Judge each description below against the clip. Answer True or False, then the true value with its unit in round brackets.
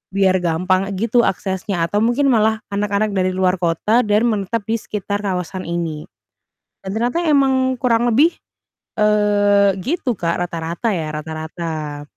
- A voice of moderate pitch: False (200 Hz)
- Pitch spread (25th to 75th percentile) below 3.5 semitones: False (4.3 semitones)